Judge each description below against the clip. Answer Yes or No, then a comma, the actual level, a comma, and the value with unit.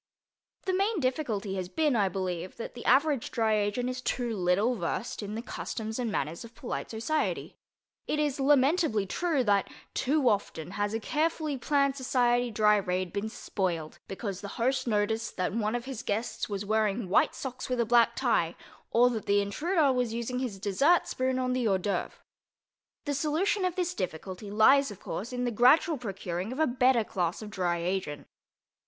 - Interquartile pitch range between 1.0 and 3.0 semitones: No, average, 4.7 semitones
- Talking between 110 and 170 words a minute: No, average, 185 wpm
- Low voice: No, high, 230 Hz